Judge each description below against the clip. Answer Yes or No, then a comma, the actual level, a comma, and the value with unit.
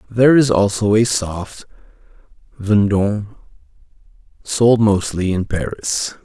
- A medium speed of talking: No, slow, 95 wpm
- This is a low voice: Yes, low, 105 Hz